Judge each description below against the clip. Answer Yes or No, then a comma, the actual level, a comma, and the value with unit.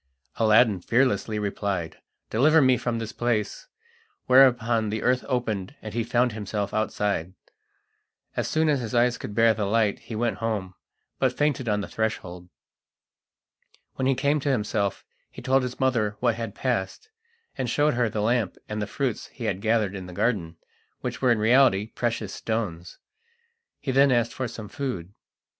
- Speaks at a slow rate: No, average, 170 wpm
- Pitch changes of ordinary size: Yes, average, 3.5 semitones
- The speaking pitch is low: Yes, low, 115 Hz